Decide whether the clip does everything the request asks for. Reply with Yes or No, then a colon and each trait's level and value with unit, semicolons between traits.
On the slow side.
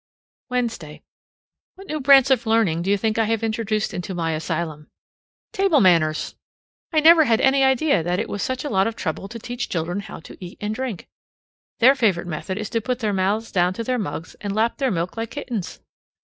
No: fast, 205 wpm